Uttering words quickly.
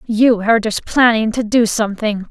No: average, 180 wpm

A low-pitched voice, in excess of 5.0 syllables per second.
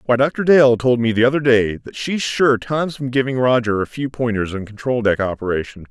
Yes: low, 125 Hz; 5.2 syllables/s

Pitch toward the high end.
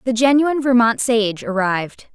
Yes: high, 230 Hz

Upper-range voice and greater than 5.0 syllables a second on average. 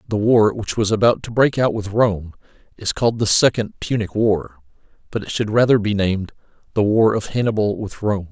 No: low, 105 Hz; 5.3 syllables/s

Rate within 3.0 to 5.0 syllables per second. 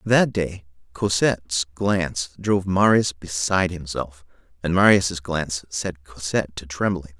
Yes: 4.6 syllables/s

